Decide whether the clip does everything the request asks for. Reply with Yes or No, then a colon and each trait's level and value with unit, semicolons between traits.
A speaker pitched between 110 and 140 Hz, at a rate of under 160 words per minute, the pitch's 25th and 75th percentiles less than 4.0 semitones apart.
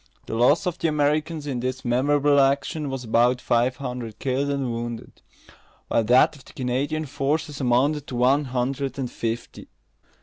No: low, 135 Hz; average, 165 wpm; average, 2.9 semitones